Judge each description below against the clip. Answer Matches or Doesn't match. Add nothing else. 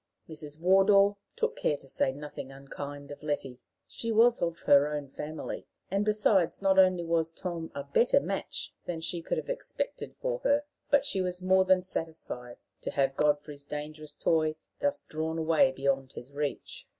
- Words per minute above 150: Matches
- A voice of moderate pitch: Matches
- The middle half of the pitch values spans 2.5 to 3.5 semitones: Doesn't match